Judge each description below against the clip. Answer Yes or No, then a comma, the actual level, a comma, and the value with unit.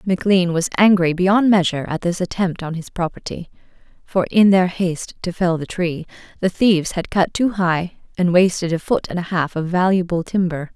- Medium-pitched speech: Yes, medium, 180 Hz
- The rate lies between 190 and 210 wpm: Yes, average, 195 wpm